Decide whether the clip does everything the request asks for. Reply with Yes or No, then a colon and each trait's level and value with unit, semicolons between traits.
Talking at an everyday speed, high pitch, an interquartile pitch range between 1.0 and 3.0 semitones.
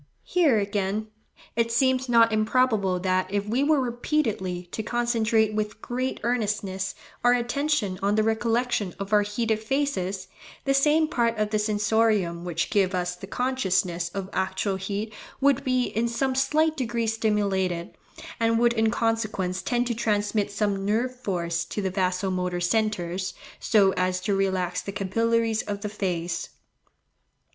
No: average, 150 wpm; high, 215 Hz; average, 3.7 semitones